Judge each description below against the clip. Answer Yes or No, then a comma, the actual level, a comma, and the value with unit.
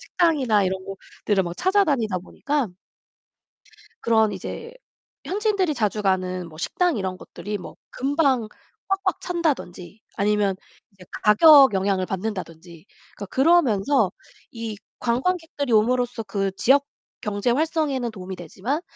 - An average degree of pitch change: No, wide, 6.9 semitones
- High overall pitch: Yes, high, 220 Hz